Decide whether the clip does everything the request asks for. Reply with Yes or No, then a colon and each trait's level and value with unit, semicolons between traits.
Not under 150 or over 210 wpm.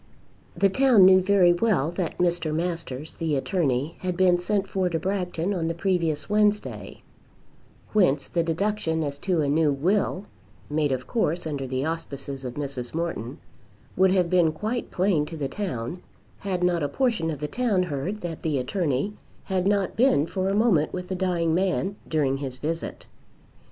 Yes: average, 175 wpm